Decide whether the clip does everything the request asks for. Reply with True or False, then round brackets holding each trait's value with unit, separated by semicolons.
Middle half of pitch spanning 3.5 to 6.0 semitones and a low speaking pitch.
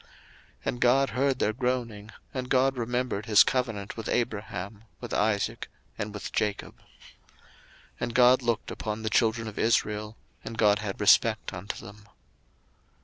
False (2.8 semitones; 110 Hz)